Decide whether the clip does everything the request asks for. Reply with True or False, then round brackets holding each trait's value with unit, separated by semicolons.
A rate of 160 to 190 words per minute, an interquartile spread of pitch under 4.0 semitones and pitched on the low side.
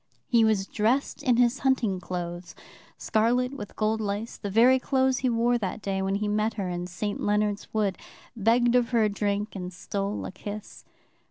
False (185 wpm; 3.1 semitones; 215 Hz)